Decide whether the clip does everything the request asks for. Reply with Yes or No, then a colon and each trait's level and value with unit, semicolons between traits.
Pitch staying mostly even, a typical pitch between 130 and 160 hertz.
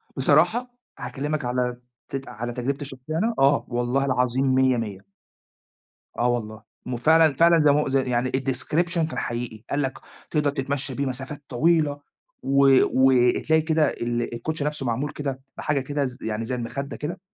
No: average, 3.3 semitones; low, 135 Hz